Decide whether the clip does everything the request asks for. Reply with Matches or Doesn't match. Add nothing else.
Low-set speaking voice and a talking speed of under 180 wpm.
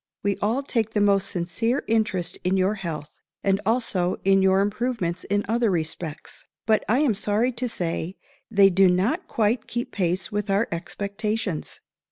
Doesn't match